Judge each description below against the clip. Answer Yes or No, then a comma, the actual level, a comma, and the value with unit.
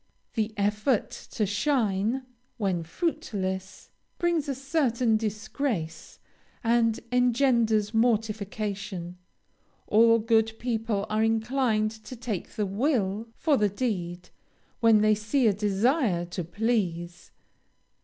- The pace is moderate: No, slow, 105 wpm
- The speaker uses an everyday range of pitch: Yes, average, 3.2 semitones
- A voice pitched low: No, high, 220 Hz